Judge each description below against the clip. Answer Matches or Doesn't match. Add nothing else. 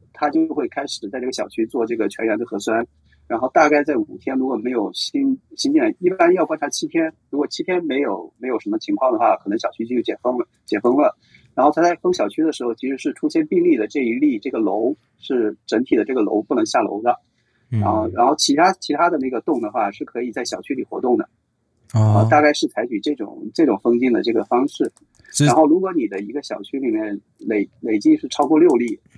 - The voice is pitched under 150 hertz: Doesn't match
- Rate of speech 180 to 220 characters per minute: Doesn't match